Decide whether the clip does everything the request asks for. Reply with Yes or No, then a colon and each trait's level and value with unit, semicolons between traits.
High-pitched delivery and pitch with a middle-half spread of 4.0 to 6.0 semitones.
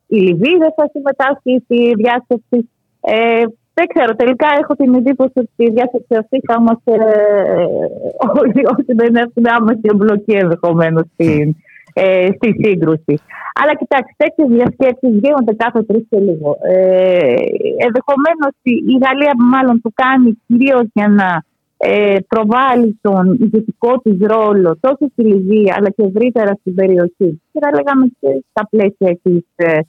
Yes: high, 230 Hz; average, 4.7 semitones